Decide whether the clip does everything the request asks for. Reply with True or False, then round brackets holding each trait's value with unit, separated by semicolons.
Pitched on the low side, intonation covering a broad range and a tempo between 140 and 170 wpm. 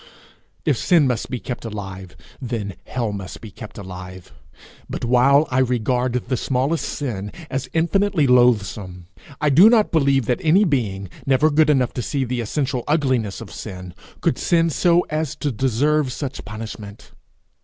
True (125 Hz; 5.7 semitones; 160 wpm)